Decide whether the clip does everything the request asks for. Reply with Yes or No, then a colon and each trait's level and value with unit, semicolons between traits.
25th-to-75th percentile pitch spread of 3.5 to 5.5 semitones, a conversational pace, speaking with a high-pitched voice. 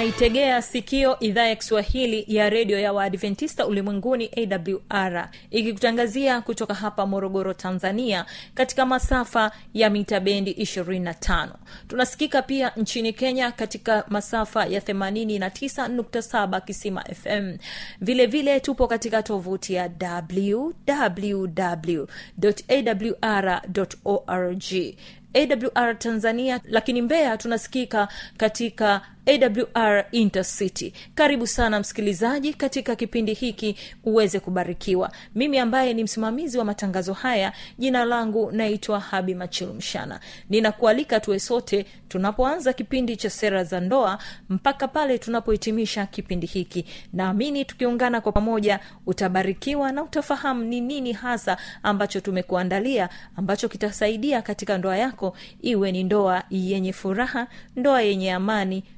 Yes: average, 3.8 semitones; average, 110 wpm; high, 215 Hz